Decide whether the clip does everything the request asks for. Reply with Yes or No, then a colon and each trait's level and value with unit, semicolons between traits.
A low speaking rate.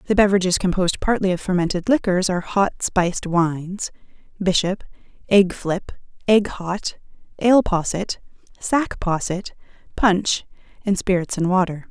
Yes: slow, 125 wpm